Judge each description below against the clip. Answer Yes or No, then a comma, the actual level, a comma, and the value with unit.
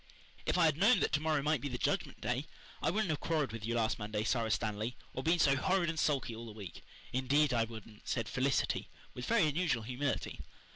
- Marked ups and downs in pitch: Yes, wide, 5.7 semitones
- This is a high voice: No, low, 135 Hz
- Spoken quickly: Yes, fast, 225 wpm